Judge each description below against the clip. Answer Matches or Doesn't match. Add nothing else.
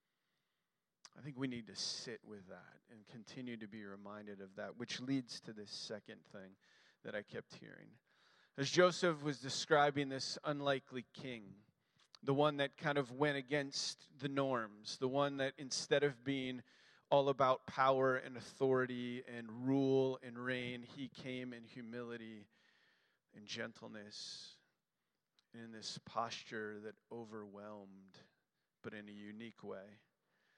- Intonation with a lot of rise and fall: Doesn't match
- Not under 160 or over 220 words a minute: Doesn't match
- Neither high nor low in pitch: Doesn't match